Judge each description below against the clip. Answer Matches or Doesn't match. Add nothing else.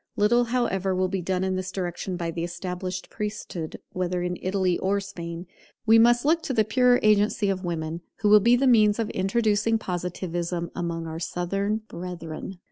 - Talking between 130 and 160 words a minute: Doesn't match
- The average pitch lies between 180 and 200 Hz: Matches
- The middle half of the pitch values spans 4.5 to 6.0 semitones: Doesn't match